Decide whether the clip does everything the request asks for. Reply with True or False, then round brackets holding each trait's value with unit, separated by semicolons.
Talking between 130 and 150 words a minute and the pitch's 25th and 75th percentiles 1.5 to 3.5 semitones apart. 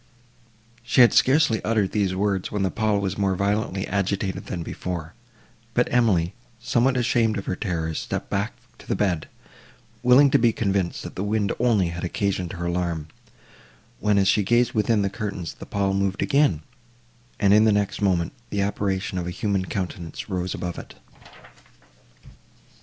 False (170 wpm; 3.1 semitones)